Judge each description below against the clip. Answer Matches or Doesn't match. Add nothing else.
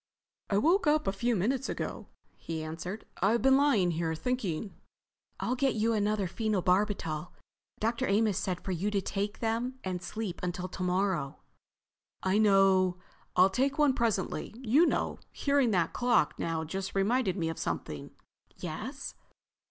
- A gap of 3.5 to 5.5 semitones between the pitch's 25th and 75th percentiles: Matches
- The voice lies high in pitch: Matches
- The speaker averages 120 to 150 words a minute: Matches